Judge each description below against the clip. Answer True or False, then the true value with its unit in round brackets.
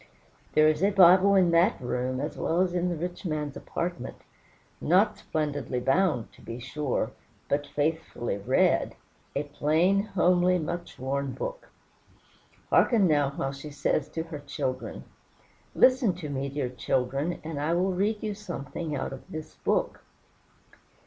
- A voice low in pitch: False (155 Hz)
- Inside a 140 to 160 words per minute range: True (150 wpm)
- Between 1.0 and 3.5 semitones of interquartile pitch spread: False (4.6 semitones)